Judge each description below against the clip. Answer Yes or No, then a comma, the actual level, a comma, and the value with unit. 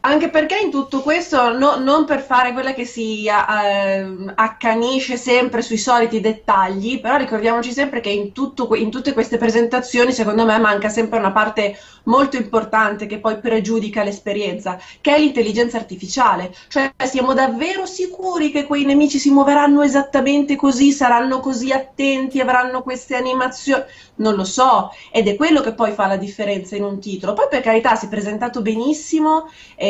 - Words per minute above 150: Yes, average, 165 wpm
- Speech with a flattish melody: No, average, 4.0 semitones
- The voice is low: No, high, 245 Hz